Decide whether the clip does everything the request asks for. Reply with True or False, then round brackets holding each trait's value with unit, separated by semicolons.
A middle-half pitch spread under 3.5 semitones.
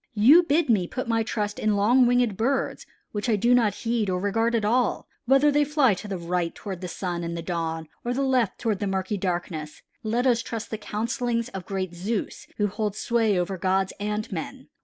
False (4.2 semitones)